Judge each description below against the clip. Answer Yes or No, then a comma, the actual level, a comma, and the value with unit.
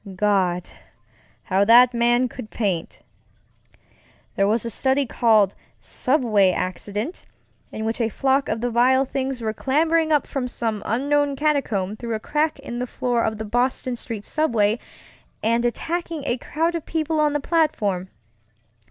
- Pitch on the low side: No, high, 240 Hz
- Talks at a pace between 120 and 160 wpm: Yes, average, 150 wpm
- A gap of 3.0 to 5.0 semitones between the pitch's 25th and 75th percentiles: Yes, average, 4.6 semitones